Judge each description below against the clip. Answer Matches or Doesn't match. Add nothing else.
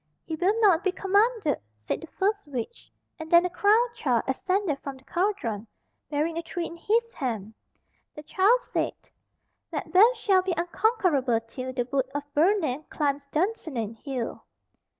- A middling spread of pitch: Doesn't match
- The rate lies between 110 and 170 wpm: Matches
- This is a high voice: Matches